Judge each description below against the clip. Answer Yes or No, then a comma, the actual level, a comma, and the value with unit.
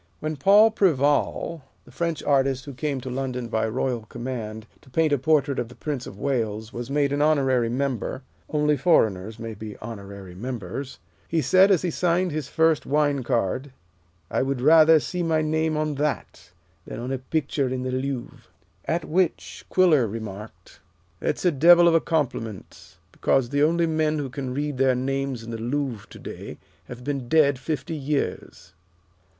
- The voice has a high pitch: No, low, 135 Hz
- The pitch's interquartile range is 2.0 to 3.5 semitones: No, average, 4.2 semitones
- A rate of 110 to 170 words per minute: No, average, 180 wpm